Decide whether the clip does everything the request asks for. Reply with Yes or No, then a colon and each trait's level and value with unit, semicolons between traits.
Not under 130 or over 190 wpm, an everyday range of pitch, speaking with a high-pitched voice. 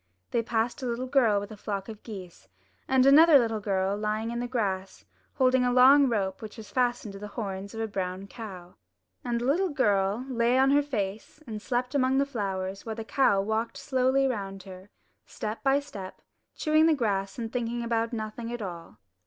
No: average, 200 wpm; average, 4.3 semitones; high, 225 Hz